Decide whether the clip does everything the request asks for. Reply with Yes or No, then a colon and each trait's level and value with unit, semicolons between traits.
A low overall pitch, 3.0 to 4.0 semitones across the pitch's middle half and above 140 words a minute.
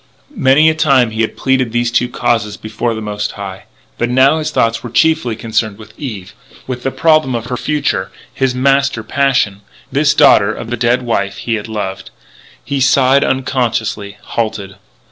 Yes: low, 120 Hz; average, 3.6 semitones; average, 175 wpm